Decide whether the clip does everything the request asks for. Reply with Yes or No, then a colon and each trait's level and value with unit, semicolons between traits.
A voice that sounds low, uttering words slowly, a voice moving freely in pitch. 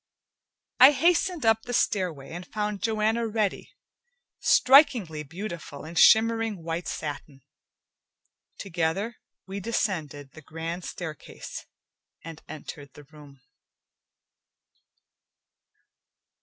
No: medium, 185 Hz; slow, 90 wpm; wide, 6.0 semitones